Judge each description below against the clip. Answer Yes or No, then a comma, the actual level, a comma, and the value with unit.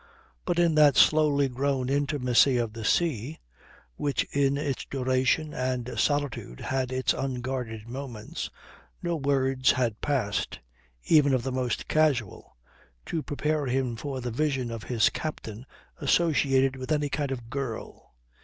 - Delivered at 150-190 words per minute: No, average, 140 wpm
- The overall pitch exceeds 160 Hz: No, low, 135 Hz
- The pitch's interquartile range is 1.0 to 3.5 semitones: Yes, average, 2.7 semitones